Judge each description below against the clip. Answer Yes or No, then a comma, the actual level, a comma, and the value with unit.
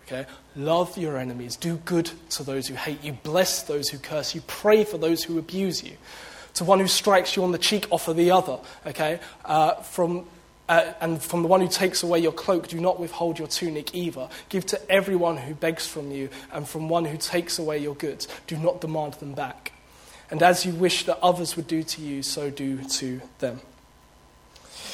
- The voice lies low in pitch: No, medium, 165 Hz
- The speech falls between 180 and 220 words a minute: Yes, fast, 205 wpm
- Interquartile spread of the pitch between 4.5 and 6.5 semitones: No, average, 3.2 semitones